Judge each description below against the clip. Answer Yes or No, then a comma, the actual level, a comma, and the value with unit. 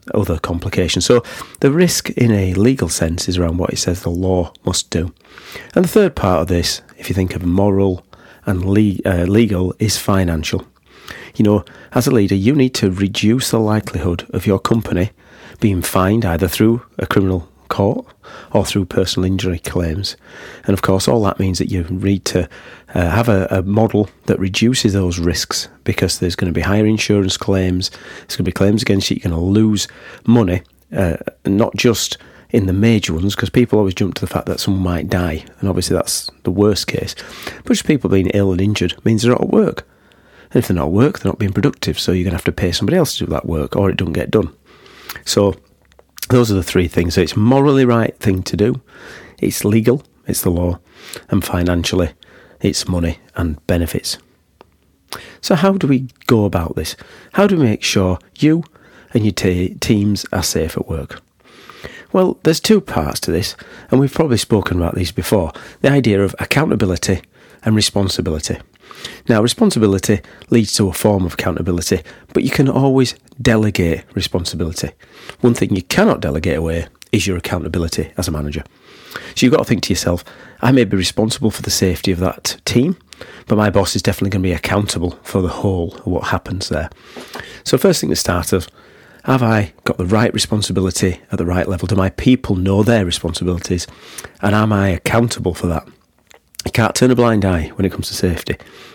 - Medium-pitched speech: No, very low, 95 Hz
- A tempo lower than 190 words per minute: No, average, 195 wpm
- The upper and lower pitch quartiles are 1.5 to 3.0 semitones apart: No, average, 3.6 semitones